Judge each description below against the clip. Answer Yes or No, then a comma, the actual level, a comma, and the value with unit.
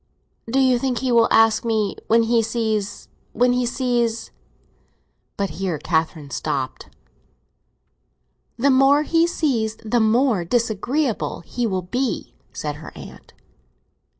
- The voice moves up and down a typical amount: Yes, average, 3.3 semitones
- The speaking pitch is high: Yes, high, 230 Hz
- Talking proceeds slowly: Yes, slow, 125 wpm